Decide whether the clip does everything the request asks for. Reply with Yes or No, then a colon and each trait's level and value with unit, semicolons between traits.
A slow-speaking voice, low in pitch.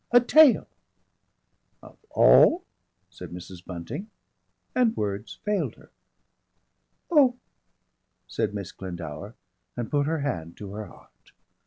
Yes: slow, 120 wpm; low, 105 Hz